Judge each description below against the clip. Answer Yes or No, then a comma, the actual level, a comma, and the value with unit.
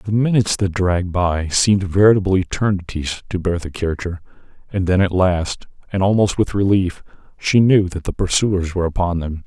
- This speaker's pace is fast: No, average, 170 wpm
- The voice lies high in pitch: No, very low, 95 Hz